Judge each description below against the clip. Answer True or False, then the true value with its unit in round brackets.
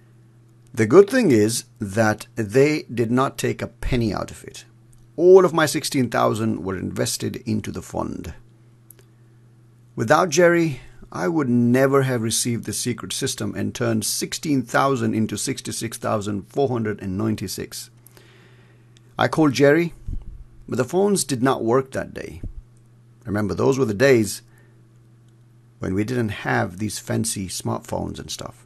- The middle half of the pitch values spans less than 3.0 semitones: True (2.5 semitones)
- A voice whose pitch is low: True (120 Hz)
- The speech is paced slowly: True (130 wpm)